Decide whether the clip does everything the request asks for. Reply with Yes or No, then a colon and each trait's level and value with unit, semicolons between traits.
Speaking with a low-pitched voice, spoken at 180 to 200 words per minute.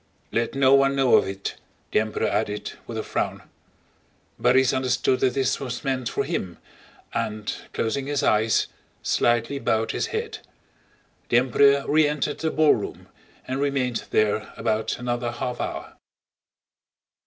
No: low, 125 Hz; average, 140 wpm